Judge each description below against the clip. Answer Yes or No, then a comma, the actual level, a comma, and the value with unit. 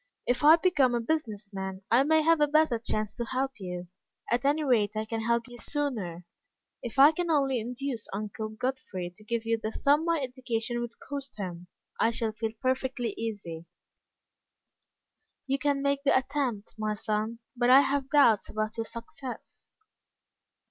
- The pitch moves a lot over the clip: No, average, 4.4 semitones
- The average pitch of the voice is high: Yes, high, 240 Hz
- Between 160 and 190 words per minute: Yes, average, 170 wpm